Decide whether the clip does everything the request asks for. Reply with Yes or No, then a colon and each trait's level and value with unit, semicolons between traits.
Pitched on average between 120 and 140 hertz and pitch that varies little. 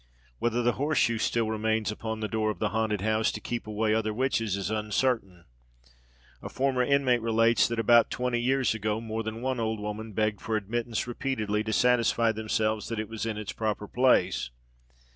No: low, 110 Hz; narrow, 1.8 semitones